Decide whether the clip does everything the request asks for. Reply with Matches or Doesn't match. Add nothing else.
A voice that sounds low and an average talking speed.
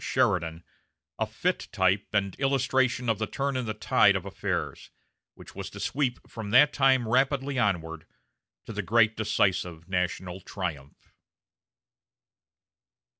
Doesn't match